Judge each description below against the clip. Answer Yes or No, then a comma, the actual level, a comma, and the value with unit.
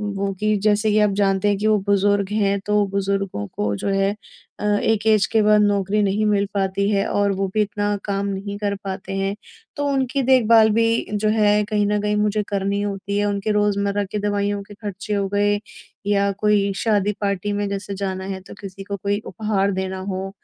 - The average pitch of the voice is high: Yes, high, 205 Hz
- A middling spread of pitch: No, narrow, 1.0 semitones